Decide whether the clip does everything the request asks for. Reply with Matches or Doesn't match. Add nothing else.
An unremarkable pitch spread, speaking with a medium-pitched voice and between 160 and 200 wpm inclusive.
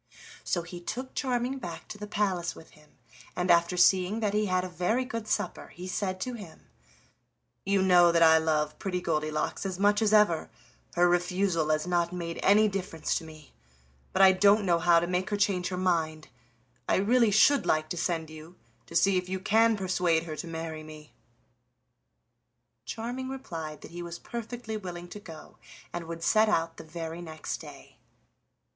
Matches